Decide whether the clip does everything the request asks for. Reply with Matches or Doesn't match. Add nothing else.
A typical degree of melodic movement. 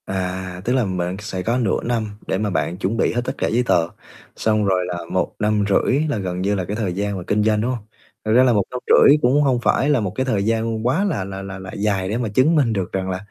Matches